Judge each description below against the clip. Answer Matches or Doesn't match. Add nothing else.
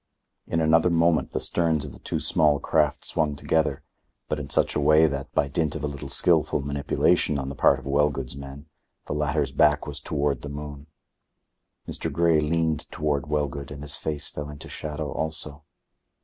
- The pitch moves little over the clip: Matches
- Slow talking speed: Doesn't match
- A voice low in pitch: Matches